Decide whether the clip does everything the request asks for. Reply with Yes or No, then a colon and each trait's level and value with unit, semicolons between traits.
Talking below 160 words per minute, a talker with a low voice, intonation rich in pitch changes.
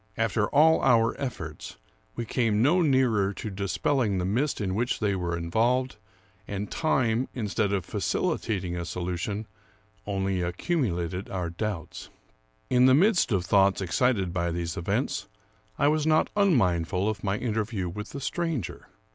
Yes: average, 145 wpm; low, 105 Hz; wide, 5.7 semitones